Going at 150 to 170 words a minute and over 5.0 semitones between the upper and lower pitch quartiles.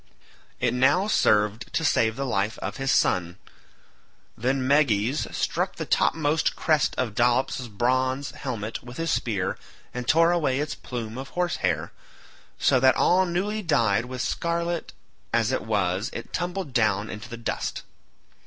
Yes: average, 155 wpm; wide, 5.5 semitones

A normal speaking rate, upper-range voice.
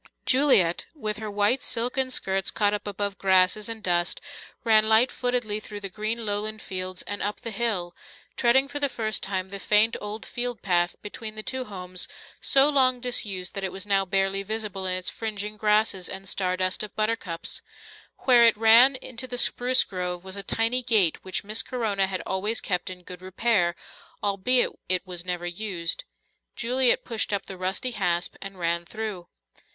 Yes: average, 180 wpm; high, 205 Hz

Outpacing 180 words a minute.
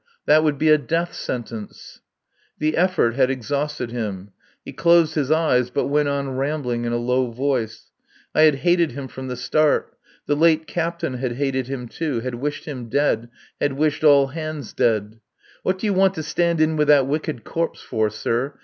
Yes: average, 190 wpm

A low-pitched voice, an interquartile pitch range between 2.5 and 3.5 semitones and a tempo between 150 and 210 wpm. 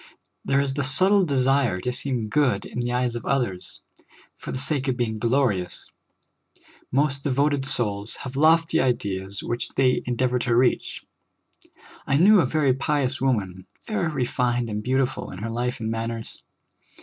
Yes: low, 125 Hz; average, 3.1 semitones; average, 160 wpm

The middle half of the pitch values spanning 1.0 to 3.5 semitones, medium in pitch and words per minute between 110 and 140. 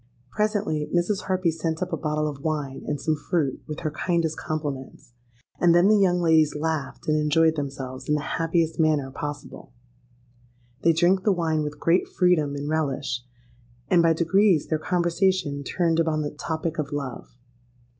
No: narrow, 2.6 semitones; medium, 160 Hz; average, 165 wpm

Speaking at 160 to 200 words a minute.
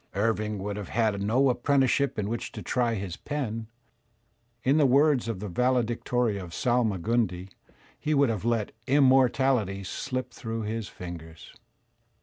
No: average, 145 wpm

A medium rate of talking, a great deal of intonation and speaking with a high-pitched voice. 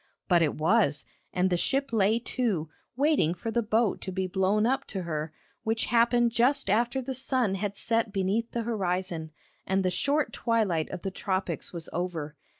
No: average, 180 wpm; average, 4.6 semitones; high, 205 Hz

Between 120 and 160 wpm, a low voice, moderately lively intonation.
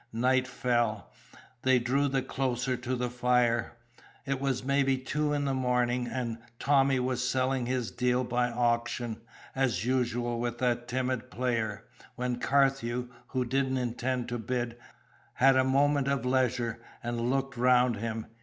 No: average, 150 wpm; low, 125 Hz; narrow, 1.6 semitones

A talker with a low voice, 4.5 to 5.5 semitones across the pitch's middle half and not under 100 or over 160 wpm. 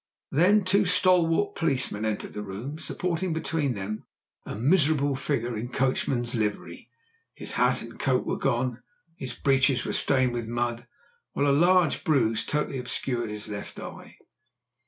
Yes: low, 130 Hz; average, 5.2 semitones; average, 155 wpm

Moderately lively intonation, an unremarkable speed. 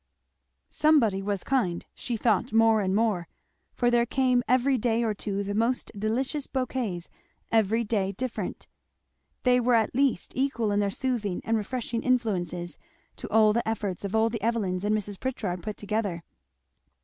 Yes: average, 3.3 semitones; average, 160 wpm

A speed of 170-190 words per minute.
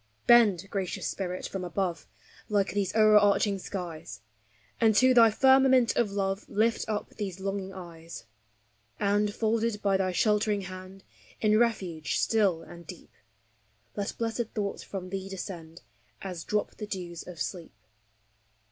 No: average, 140 wpm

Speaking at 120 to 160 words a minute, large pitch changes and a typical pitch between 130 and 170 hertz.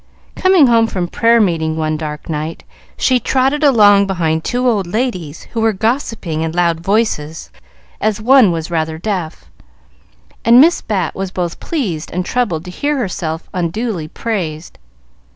No: average, 150 wpm; wide, 6.2 semitones; high, 190 Hz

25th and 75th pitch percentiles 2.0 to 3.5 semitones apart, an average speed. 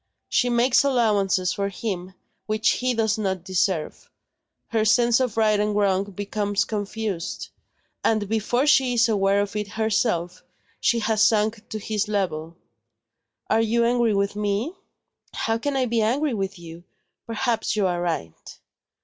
Yes: average, 2.7 semitones; average, 150 wpm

